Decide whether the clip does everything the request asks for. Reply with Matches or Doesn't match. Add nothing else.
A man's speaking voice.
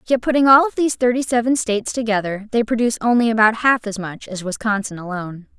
Doesn't match